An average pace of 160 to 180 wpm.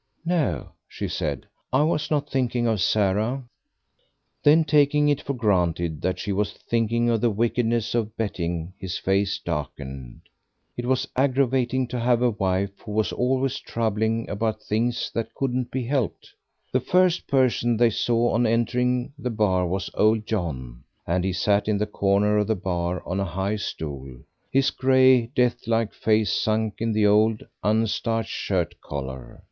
Yes: average, 165 wpm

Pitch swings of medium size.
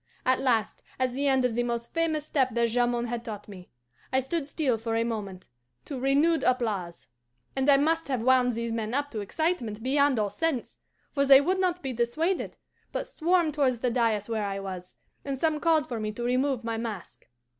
Yes: average, 4.0 semitones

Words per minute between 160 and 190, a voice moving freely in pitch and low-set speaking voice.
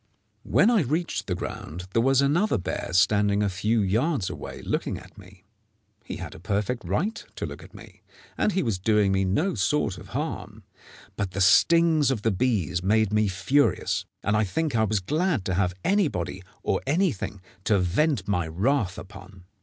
Yes: average, 185 wpm; wide, 7.0 semitones; low, 105 Hz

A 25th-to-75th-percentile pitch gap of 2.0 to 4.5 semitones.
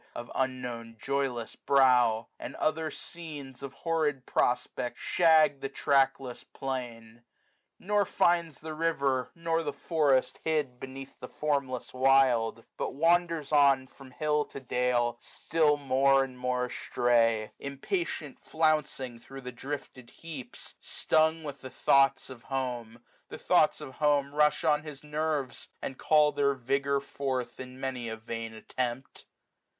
Yes: average, 3.1 semitones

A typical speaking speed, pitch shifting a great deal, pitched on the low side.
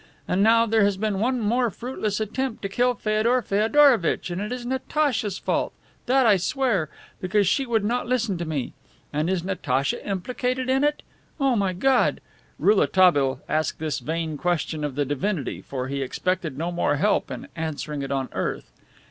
No: average, 175 wpm; wide, 7.2 semitones; high, 200 Hz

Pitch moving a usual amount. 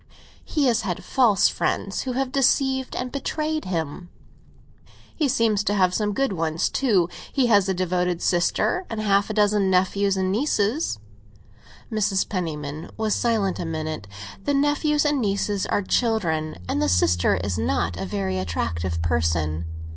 No: wide, 7.0 semitones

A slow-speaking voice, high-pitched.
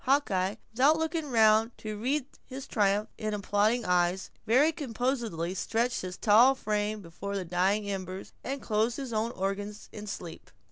No: average, 155 wpm; high, 215 Hz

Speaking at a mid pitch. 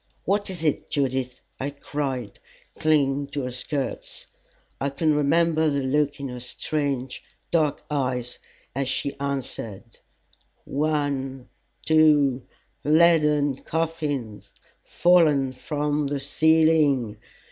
Yes: medium, 145 Hz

